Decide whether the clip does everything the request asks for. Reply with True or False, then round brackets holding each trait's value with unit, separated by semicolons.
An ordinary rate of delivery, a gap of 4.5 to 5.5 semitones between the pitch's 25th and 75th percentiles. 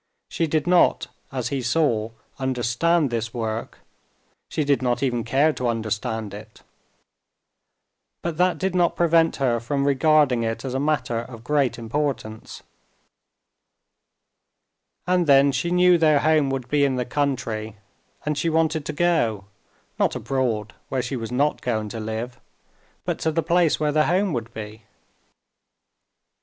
True (150 wpm; 4.9 semitones)